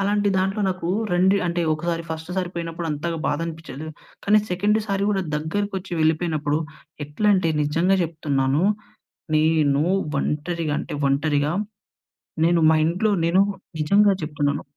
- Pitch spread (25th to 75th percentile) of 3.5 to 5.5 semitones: Yes, average, 3.8 semitones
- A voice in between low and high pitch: Yes, medium, 165 Hz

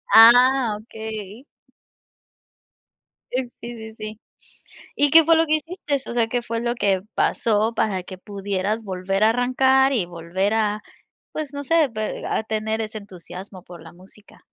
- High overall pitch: Yes, high, 220 Hz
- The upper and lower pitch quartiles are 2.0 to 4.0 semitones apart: Yes, average, 3.6 semitones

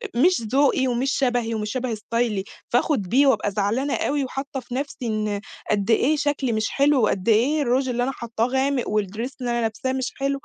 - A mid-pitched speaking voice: No, high, 245 Hz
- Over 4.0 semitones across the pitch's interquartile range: No, average, 3.6 semitones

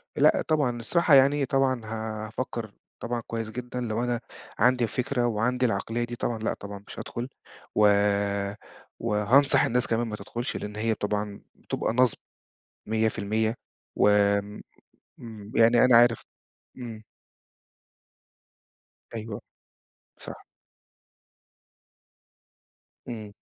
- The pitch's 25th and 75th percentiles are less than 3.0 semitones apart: Yes, narrow, 2.4 semitones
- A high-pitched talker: No, low, 115 Hz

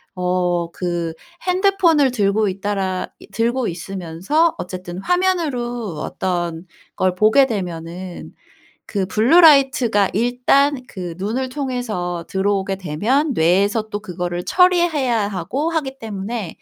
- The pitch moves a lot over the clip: Yes, wide, 6.6 semitones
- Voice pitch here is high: Yes, high, 205 Hz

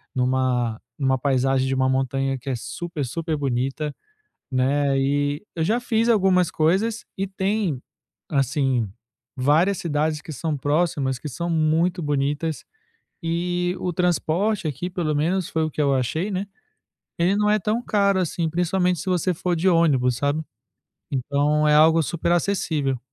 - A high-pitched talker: No, medium, 155 Hz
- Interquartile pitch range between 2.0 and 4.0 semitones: No, average, 4.6 semitones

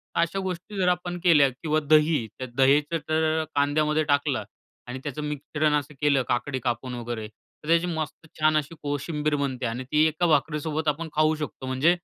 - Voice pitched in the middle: Yes, medium, 150 Hz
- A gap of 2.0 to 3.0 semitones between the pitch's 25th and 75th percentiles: Yes, narrow, 2.4 semitones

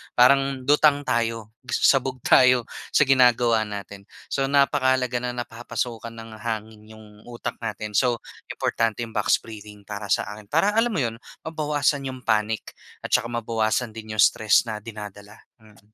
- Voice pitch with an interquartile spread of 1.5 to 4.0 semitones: Yes, average, 3.2 semitones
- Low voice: Yes, low, 115 Hz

